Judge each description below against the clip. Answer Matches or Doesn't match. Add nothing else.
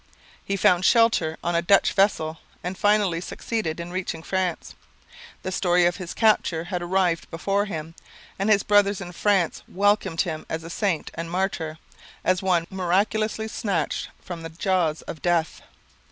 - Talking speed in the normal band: Matches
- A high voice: Doesn't match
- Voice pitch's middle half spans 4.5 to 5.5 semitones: Doesn't match